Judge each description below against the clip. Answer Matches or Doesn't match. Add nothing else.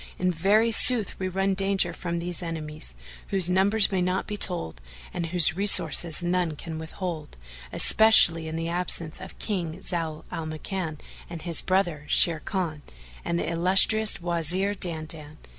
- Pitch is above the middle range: Doesn't match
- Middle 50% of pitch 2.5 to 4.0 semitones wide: Matches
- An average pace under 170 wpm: Matches